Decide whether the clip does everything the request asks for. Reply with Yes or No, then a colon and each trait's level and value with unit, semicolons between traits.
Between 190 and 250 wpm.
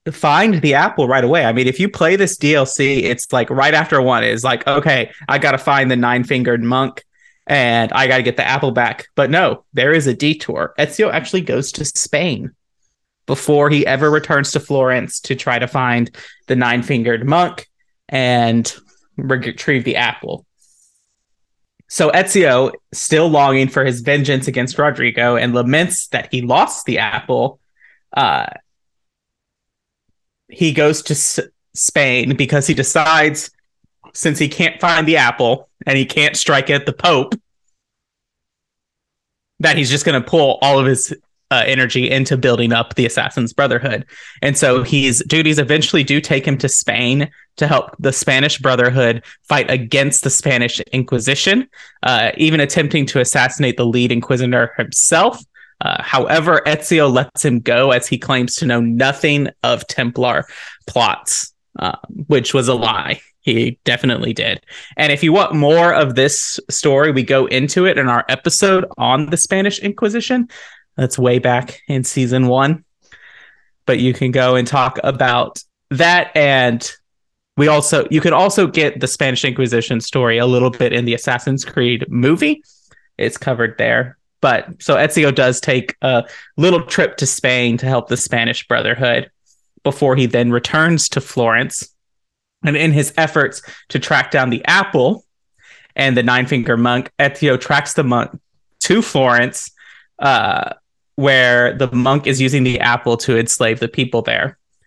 No: average, 160 wpm